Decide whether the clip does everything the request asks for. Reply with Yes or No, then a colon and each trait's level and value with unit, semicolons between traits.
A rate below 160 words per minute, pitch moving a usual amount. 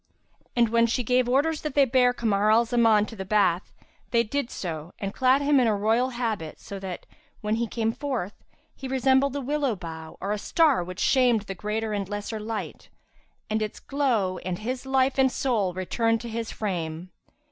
No: average, 195 wpm; average, 4.3 semitones